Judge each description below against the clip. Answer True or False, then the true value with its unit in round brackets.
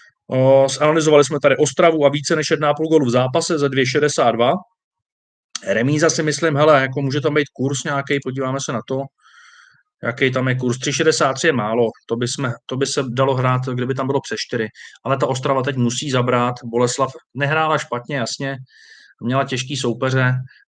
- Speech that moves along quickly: True (175 wpm)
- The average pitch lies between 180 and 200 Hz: False (135 Hz)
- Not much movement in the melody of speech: False (3.0 semitones)